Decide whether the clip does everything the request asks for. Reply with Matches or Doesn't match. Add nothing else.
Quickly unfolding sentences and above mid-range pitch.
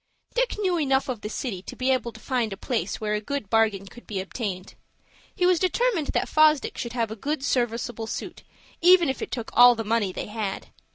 Matches